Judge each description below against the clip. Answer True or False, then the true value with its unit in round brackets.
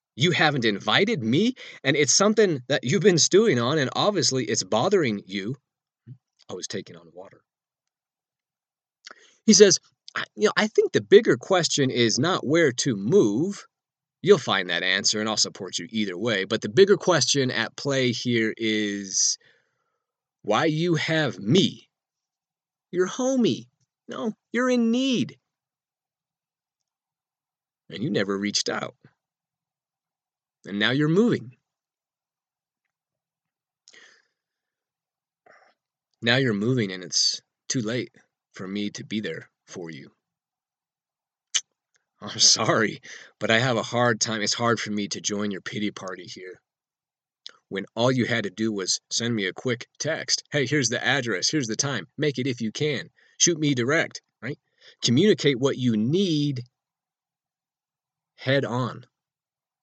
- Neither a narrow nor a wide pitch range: False (6.4 semitones)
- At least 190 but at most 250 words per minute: False (140 wpm)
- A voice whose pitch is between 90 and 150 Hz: True (135 Hz)